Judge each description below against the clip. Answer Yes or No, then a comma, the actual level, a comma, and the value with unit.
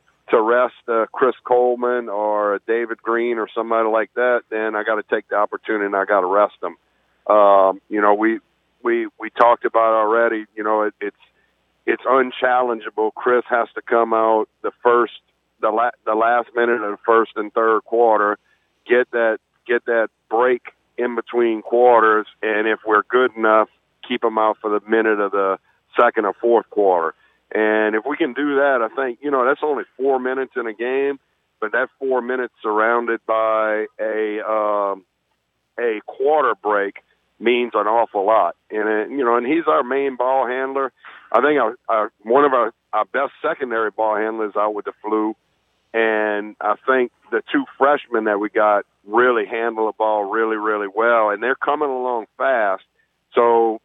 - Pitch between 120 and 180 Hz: No, low, 110 Hz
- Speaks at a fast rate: No, average, 185 wpm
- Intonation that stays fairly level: Yes, narrow, 2.2 semitones